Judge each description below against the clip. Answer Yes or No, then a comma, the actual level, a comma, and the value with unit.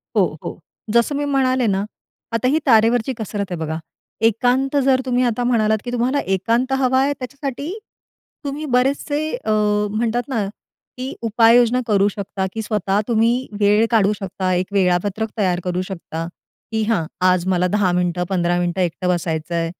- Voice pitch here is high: Yes, high, 220 Hz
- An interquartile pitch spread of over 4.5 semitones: Yes, average, 5.3 semitones